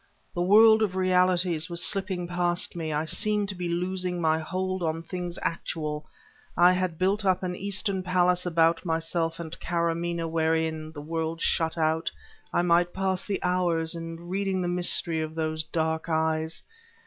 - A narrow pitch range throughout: Yes, narrow, 2.1 semitones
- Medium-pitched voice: Yes, medium, 175 Hz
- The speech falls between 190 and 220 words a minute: No, average, 165 wpm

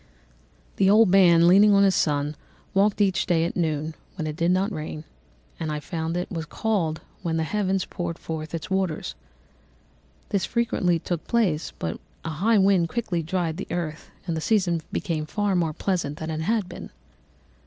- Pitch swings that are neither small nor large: Yes, average, 3.4 semitones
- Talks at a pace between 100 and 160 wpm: No, average, 180 wpm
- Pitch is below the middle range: No, medium, 175 Hz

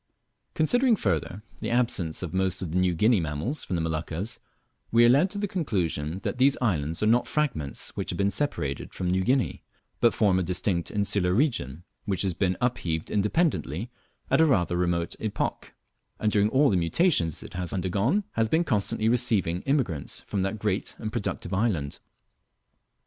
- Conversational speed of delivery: Yes, average, 175 wpm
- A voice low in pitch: Yes, low, 100 Hz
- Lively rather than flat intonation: Yes, wide, 5.8 semitones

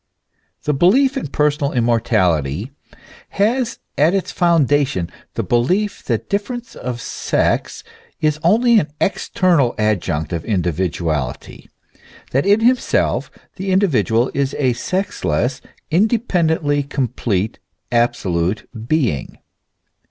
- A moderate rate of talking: No, slow, 105 wpm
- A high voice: No, medium, 140 Hz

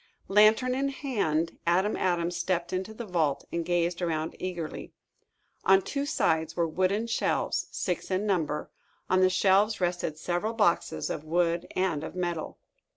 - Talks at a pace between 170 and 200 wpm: No, average, 155 wpm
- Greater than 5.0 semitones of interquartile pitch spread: No, average, 3.1 semitones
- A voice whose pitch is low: No, medium, 180 Hz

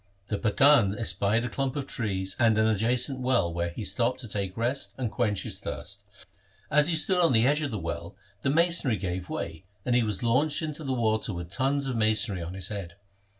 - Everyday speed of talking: No, fast, 215 wpm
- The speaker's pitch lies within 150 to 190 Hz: No, low, 115 Hz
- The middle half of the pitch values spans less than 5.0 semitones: No, average, 5.3 semitones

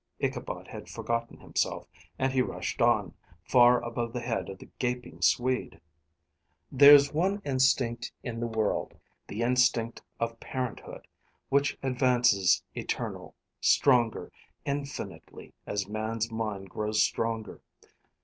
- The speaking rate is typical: No, slow, 120 wpm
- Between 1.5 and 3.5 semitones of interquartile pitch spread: Yes, narrow, 2.5 semitones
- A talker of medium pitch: No, low, 120 Hz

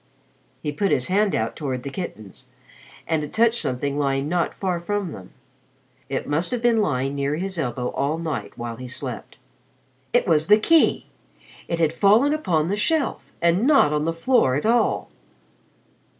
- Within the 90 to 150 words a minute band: No, average, 175 wpm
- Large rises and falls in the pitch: Yes, wide, 6.8 semitones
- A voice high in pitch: No, medium, 160 Hz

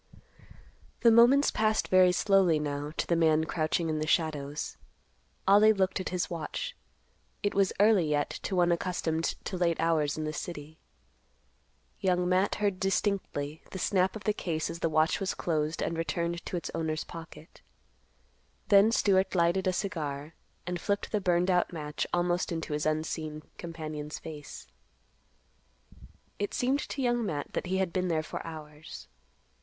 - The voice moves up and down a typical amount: Yes, average, 3.4 semitones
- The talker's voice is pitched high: No, medium, 170 Hz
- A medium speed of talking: Yes, average, 160 wpm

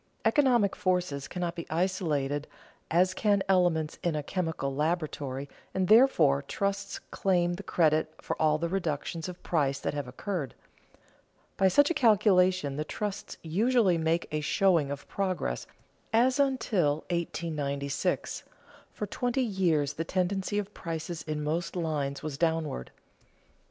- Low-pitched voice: No, medium, 170 Hz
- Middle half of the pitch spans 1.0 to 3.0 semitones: No, average, 4.3 semitones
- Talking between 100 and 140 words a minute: Yes, slow, 135 wpm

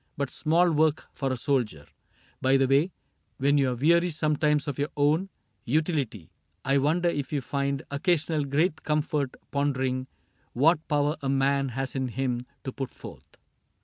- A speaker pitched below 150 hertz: Yes, medium, 140 Hz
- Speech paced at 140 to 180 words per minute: Yes, average, 160 wpm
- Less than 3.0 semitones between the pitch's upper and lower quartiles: Yes, narrow, 2.4 semitones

